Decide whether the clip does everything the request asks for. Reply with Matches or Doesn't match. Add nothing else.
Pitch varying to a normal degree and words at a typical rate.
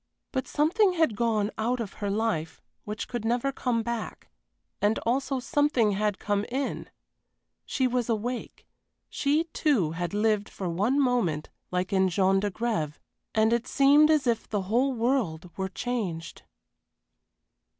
Matches